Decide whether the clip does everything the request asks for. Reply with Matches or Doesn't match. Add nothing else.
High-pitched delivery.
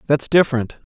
Doesn't match